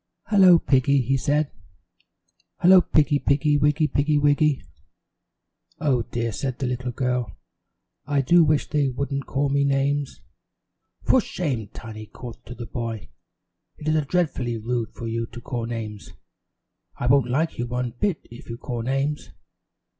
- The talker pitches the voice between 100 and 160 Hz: Yes, low, 135 Hz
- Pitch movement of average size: Yes, average, 3.7 semitones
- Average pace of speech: Yes, average, 150 wpm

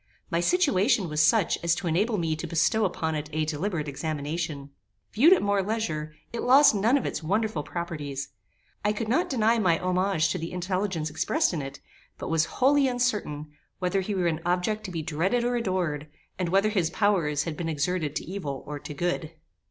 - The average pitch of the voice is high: No, medium, 175 Hz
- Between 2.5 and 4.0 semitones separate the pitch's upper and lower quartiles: No, average, 5.2 semitones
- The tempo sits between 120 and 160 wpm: No, average, 195 wpm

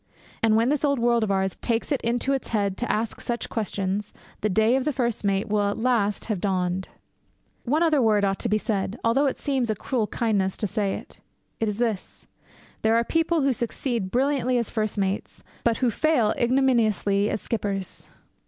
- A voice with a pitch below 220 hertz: No, high, 225 Hz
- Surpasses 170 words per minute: Yes, average, 200 wpm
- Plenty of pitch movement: No, average, 3.6 semitones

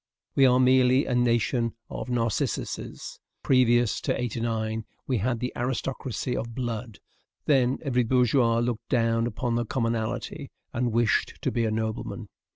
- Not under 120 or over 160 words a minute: Yes, average, 145 wpm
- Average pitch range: No, narrow, 1.7 semitones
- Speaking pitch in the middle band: No, low, 120 Hz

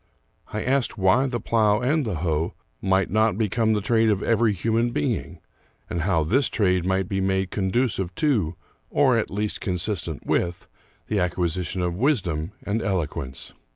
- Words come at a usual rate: Yes, average, 160 wpm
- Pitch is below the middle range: Yes, very low, 95 Hz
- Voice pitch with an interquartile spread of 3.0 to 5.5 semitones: Yes, average, 4.0 semitones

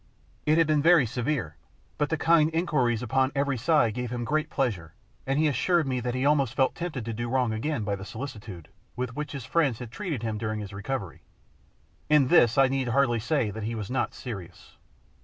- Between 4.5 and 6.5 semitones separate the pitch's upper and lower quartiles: Yes, average, 4.9 semitones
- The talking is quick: Yes, fast, 210 wpm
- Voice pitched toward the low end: Yes, low, 125 Hz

